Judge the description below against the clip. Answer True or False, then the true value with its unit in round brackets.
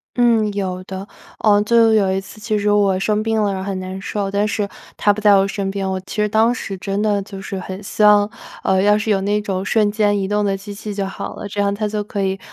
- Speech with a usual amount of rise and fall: False (1.4 semitones)